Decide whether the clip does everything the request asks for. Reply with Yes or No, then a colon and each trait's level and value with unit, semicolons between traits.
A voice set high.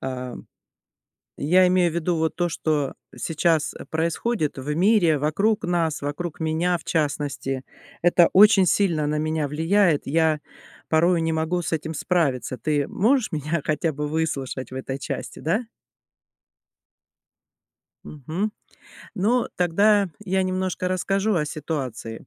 No: medium, 160 Hz